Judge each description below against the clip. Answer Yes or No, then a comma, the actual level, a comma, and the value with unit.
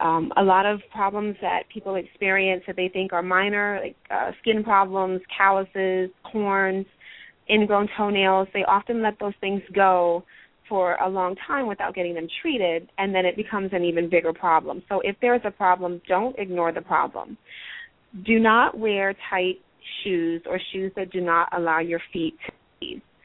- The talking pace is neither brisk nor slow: Yes, average, 175 wpm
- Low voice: No, high, 190 Hz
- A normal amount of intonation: No, narrow, 2.2 semitones